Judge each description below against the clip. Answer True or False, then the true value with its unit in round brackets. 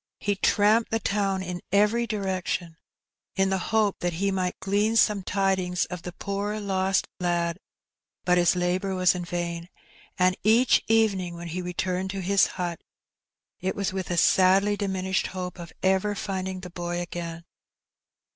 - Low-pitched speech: False (190 Hz)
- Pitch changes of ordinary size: False (2.0 semitones)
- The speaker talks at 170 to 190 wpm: False (160 wpm)